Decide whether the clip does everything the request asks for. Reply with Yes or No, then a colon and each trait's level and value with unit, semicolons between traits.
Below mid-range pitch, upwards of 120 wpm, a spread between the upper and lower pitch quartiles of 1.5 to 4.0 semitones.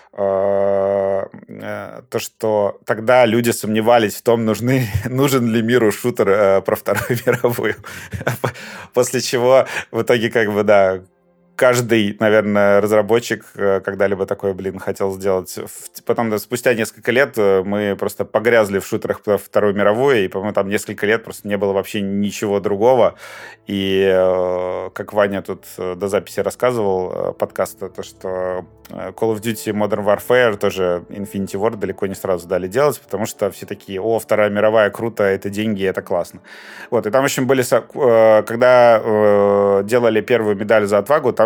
Yes: low, 105 Hz; average, 150 wpm; average, 2.8 semitones